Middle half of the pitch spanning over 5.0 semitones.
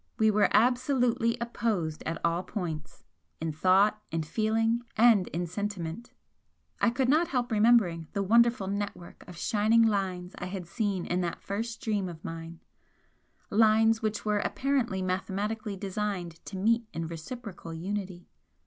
No: average, 4.1 semitones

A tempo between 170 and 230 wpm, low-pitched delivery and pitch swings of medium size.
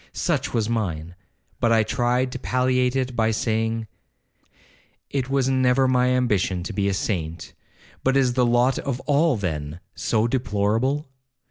No: average, 150 wpm; low, 120 Hz; average, 3.4 semitones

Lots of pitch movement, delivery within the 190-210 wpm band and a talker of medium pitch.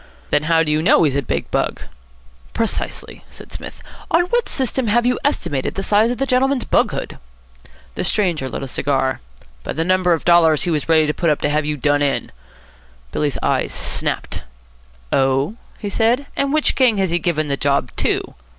Yes: wide, 7.6 semitones; average, 195 wpm; medium, 170 Hz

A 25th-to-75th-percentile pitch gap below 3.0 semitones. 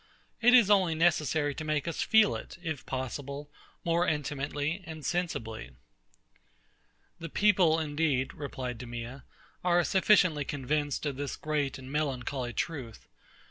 No: average, 3.8 semitones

